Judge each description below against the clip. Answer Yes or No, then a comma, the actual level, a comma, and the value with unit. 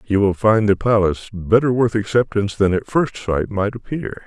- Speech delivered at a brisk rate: No, average, 195 wpm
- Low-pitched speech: Yes, low, 105 Hz